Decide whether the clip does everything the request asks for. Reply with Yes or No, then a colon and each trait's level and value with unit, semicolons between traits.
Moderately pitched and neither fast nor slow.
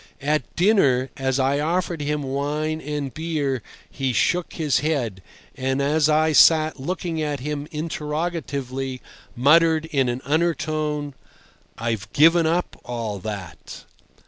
No: medium, 150 Hz; slow, 125 wpm